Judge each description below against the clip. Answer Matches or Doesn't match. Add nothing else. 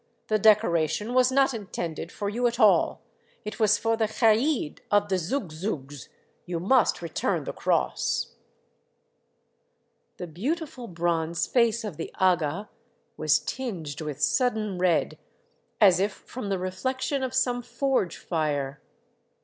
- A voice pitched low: Doesn't match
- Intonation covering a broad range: Matches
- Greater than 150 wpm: Doesn't match